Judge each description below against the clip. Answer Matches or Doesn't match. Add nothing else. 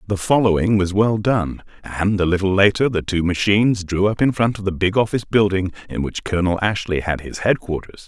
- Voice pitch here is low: Matches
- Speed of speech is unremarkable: Doesn't match